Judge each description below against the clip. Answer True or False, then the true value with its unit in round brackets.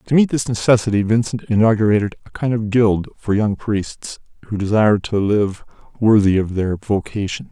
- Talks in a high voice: False (105 Hz)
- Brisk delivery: False (170 wpm)